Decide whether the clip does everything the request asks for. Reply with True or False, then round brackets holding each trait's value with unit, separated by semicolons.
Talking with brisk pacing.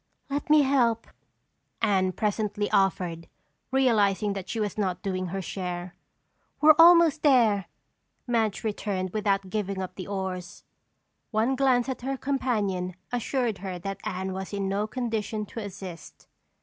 False (140 wpm)